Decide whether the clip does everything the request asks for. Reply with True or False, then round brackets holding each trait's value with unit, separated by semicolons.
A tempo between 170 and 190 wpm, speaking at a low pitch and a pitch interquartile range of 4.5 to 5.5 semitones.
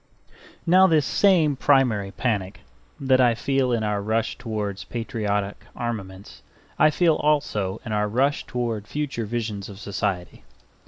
False (140 wpm; 115 Hz; 4.8 semitones)